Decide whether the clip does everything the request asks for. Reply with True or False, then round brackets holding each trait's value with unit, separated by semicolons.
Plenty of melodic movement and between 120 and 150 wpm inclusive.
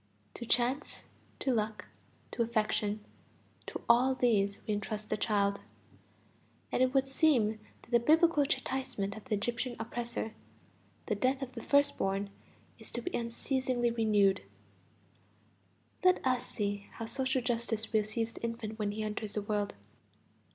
False (3.3 semitones; 145 wpm)